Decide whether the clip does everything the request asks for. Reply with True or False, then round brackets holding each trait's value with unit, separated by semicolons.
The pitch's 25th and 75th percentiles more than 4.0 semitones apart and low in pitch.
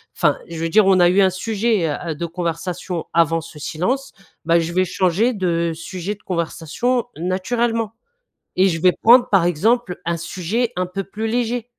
False (4.8 semitones; 185 Hz)